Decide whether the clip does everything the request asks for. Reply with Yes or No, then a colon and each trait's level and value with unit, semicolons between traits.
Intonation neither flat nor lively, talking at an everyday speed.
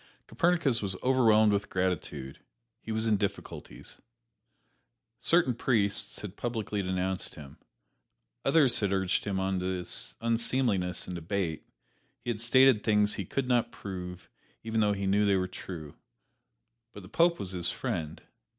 Yes: average, 4.0 semitones; average, 145 wpm